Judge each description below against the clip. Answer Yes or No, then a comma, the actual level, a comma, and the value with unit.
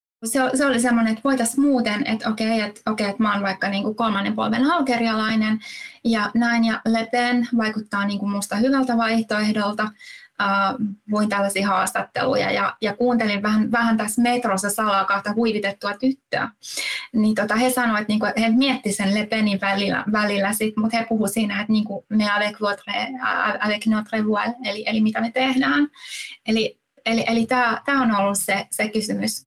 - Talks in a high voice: Yes, high, 220 Hz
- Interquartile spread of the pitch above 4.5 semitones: No, average, 2.7 semitones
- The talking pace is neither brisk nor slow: No, fast, 175 wpm